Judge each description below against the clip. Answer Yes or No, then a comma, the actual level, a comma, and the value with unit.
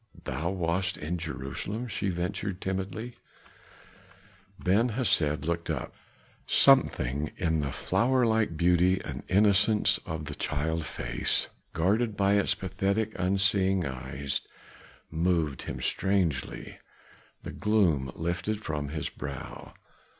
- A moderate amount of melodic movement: Yes, average, 4.6 semitones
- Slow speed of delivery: Yes, slow, 115 wpm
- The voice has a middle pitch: No, very low, 90 Hz